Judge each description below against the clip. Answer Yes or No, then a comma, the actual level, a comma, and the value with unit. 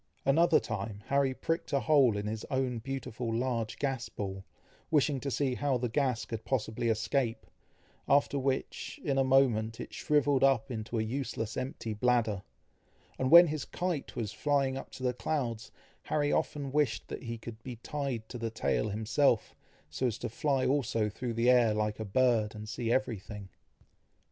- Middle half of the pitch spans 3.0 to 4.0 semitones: Yes, average, 3.7 semitones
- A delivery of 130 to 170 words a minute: No, average, 180 wpm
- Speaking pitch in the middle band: No, low, 125 Hz